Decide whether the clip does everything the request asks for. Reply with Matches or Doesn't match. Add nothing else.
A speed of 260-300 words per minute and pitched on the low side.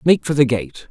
Matches